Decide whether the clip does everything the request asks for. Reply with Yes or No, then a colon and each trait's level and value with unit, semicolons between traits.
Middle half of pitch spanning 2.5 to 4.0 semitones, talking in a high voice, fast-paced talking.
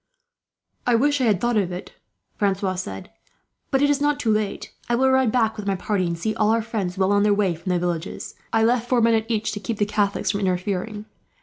Yes: average, 3.4 semitones; high, 210 Hz; fast, 240 wpm